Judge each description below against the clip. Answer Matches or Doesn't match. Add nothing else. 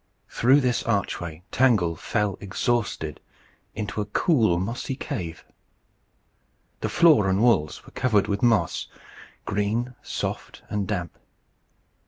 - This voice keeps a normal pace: Doesn't match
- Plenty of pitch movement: Doesn't match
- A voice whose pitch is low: Matches